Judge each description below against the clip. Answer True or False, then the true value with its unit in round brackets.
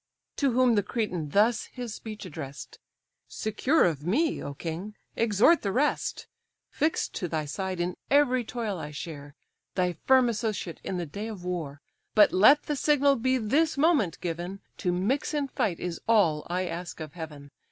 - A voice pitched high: True (200 Hz)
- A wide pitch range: True (6.6 semitones)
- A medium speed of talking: True (175 wpm)